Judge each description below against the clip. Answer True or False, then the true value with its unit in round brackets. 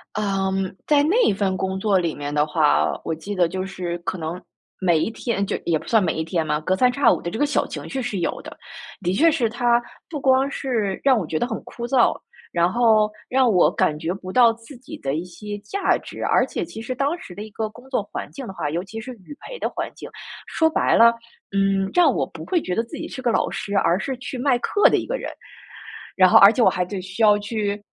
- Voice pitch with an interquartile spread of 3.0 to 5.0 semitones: False (5.4 semitones)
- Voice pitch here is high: True (205 Hz)